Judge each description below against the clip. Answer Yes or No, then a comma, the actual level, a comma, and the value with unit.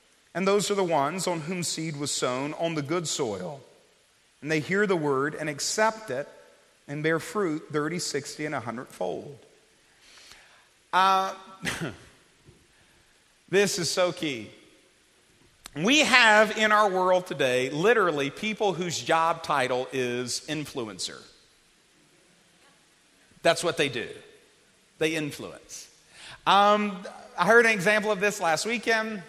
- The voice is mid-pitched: Yes, medium, 180 Hz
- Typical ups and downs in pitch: No, wide, 5.7 semitones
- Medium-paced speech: No, slow, 130 wpm